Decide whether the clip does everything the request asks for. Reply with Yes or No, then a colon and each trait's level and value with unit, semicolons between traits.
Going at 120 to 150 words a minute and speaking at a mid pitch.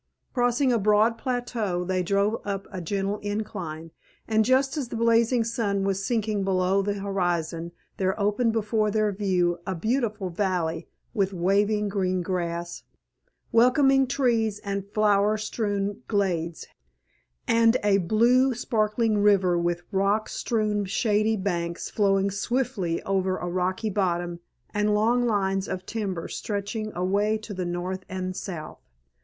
No: average, 140 wpm; high, 200 Hz